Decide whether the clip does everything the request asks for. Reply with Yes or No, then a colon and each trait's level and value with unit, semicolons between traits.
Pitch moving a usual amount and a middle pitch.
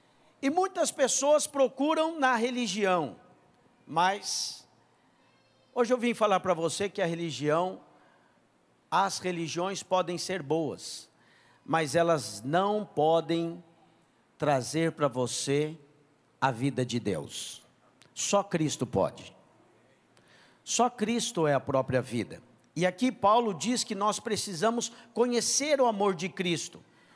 No: wide, 7.5 semitones; medium, 180 Hz